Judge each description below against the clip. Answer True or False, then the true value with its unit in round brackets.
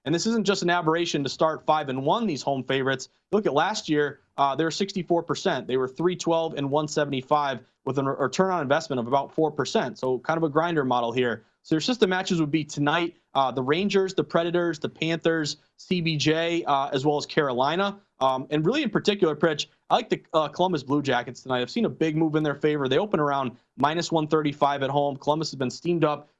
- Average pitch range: True (3.5 semitones)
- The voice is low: False (155 Hz)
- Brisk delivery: True (220 wpm)